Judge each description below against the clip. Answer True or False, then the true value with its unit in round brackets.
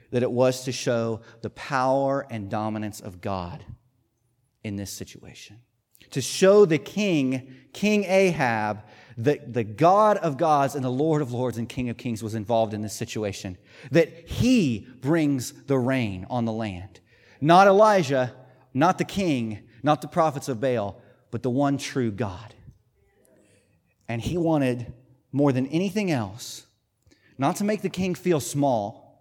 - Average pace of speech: True (155 wpm)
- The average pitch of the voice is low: True (125 Hz)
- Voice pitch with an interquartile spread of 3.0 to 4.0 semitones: False (4.6 semitones)